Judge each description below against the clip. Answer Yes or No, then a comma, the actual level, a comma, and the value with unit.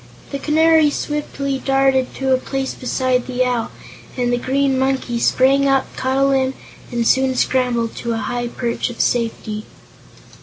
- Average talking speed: Yes, average, 160 wpm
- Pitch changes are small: Yes, narrow, 1.9 semitones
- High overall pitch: Yes, very high, 260 Hz